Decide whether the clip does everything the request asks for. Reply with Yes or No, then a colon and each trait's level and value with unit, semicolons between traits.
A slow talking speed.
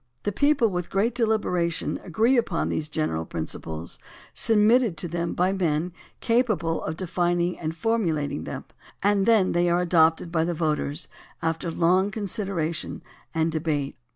No: average, 150 wpm